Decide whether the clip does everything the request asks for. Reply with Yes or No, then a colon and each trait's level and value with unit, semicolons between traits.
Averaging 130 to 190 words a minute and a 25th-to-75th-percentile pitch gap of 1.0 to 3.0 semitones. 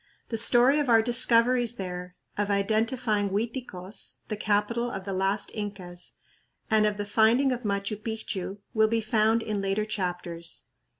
Yes: average, 155 wpm; average, 2.7 semitones